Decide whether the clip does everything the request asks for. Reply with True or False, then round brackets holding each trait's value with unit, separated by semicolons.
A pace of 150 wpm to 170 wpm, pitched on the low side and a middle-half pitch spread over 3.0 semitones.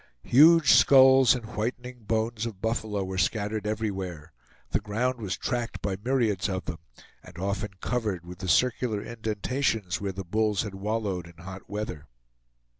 True (160 wpm; 105 Hz; 3.7 semitones)